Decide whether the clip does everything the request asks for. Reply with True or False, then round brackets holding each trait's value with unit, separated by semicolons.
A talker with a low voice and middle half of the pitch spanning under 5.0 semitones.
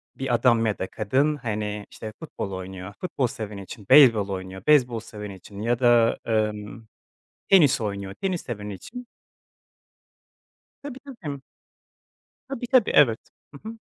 False (115 Hz; 5.4 semitones)